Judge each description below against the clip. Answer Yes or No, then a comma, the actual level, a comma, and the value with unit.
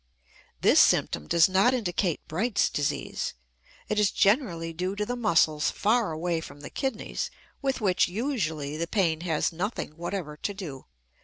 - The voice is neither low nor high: Yes, medium, 180 Hz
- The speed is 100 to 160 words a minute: Yes, average, 155 wpm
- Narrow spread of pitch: No, average, 4.9 semitones